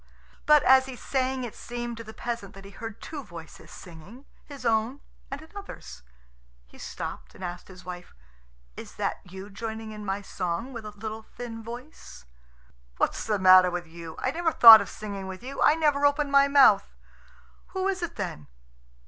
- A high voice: Yes, high, 225 Hz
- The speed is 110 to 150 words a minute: No, average, 180 wpm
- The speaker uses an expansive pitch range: Yes, wide, 5.8 semitones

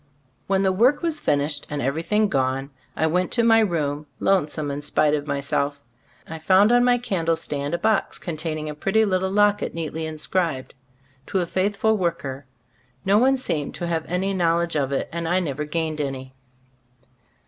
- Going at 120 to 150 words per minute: No, average, 175 wpm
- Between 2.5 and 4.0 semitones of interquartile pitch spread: No, average, 4.8 semitones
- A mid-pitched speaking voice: Yes, medium, 165 Hz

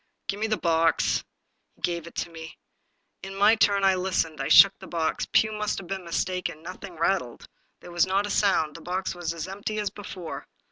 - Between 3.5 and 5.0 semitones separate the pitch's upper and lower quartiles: No, average, 2.8 semitones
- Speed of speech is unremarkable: No, fast, 215 wpm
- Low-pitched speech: No, medium, 185 Hz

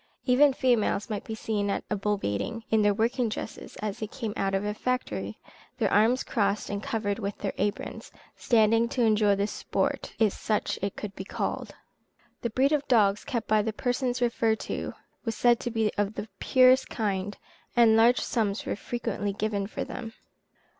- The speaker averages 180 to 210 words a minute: Yes, average, 190 wpm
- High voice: Yes, high, 220 Hz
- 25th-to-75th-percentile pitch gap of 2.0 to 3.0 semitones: Yes, narrow, 2.6 semitones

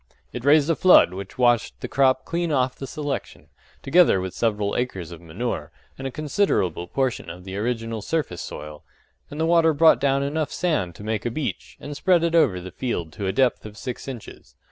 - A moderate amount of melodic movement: No, wide, 7.3 semitones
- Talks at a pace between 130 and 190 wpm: No, fast, 205 wpm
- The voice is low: Yes, low, 125 Hz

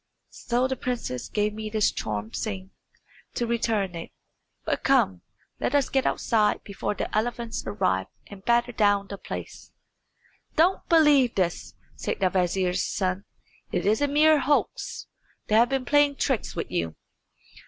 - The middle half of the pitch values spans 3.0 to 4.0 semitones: No, average, 5.1 semitones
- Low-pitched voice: No, high, 220 Hz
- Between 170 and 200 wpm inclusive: No, average, 155 wpm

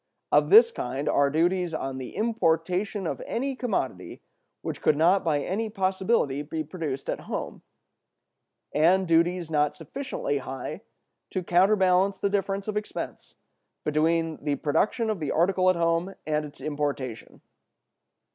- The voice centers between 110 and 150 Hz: No, medium, 170 Hz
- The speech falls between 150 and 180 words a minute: No, average, 140 wpm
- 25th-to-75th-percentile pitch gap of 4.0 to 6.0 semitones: Yes, average, 4.7 semitones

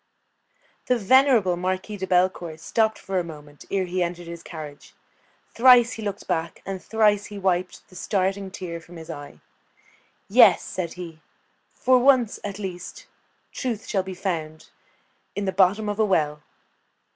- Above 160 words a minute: No, average, 155 wpm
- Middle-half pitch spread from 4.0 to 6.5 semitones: No, average, 3.4 semitones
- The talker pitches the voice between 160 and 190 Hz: Yes, medium, 185 Hz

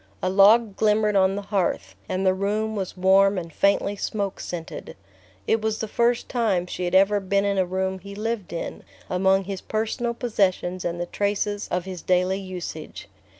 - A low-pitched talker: No, high, 195 Hz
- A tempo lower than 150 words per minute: No, average, 185 wpm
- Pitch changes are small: Yes, narrow, 2.1 semitones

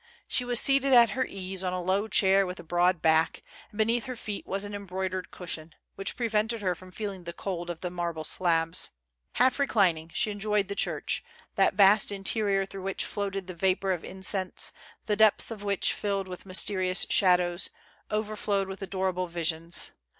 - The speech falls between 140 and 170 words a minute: No, average, 185 wpm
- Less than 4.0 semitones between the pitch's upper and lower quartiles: Yes, narrow, 2.4 semitones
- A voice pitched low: No, high, 195 Hz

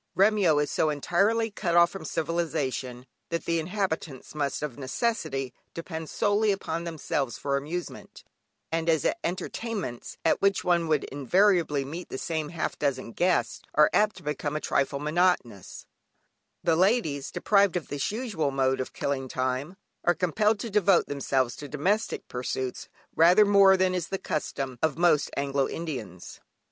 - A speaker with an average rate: Yes, average, 155 wpm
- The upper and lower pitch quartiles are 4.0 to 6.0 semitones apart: Yes, average, 5.1 semitones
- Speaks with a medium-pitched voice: Yes, medium, 160 Hz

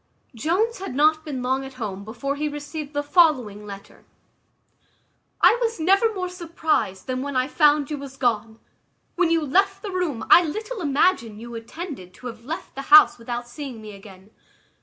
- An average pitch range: No, wide, 6.0 semitones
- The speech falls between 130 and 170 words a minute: No, average, 180 wpm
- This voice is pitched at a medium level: No, very high, 285 Hz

